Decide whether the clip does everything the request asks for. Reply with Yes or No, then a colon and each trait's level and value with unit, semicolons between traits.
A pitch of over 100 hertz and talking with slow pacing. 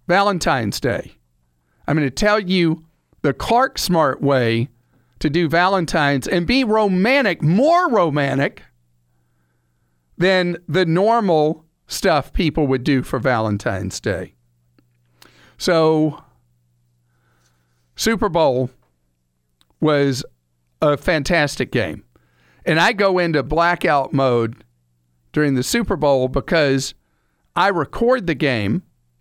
Yes: low, 135 Hz; slow, 105 wpm